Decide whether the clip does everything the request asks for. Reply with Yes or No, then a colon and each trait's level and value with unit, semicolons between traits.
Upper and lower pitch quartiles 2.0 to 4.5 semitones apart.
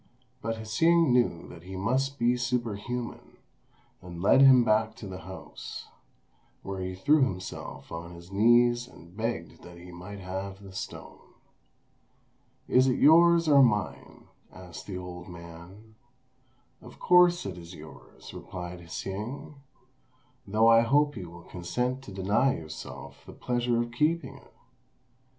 No: wide, 5.5 semitones